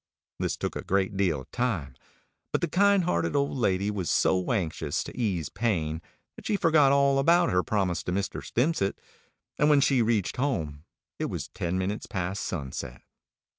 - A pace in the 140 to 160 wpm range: No, average, 175 wpm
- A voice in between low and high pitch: No, low, 100 Hz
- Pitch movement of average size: No, wide, 7.8 semitones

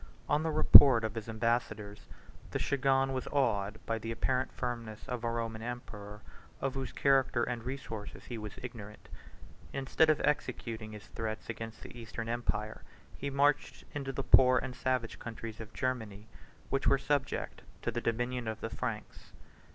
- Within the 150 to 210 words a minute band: Yes, average, 165 wpm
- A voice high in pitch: No, low, 120 Hz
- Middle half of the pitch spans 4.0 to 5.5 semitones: No, average, 3.1 semitones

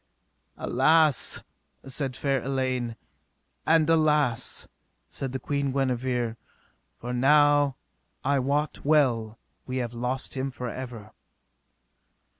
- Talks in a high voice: No, low, 130 Hz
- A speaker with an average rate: No, slow, 100 wpm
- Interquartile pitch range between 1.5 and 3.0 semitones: Yes, average, 2.7 semitones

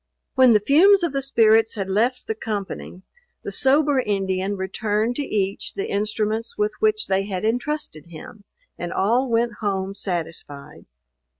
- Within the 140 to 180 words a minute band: Yes, average, 155 wpm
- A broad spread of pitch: No, average, 3.9 semitones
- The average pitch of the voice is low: No, high, 215 Hz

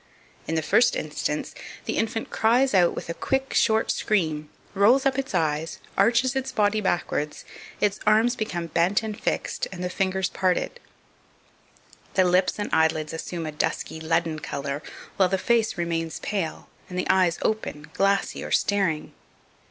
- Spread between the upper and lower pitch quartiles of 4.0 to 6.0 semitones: Yes, average, 5.1 semitones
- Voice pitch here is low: No, medium, 185 Hz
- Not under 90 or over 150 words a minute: No, average, 160 wpm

